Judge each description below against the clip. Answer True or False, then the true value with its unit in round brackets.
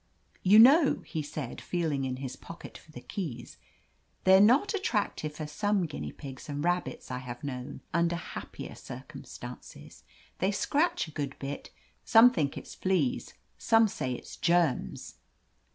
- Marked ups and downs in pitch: True (6.7 semitones)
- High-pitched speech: False (170 Hz)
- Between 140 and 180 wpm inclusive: True (150 wpm)